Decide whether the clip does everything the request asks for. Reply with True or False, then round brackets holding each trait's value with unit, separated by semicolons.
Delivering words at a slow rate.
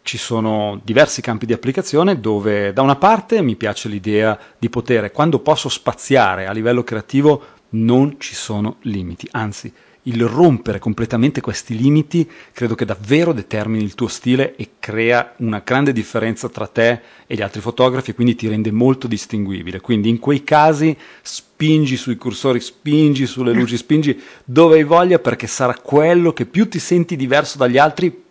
False (165 wpm)